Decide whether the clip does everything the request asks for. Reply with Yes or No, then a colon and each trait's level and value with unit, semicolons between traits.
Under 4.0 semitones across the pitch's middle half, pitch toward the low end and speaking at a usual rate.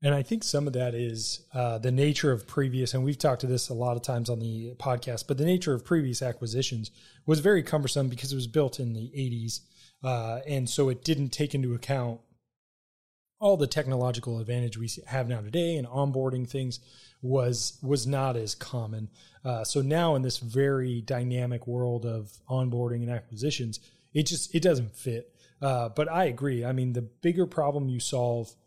Yes: average, 2.9 semitones; low, 125 Hz; average, 195 wpm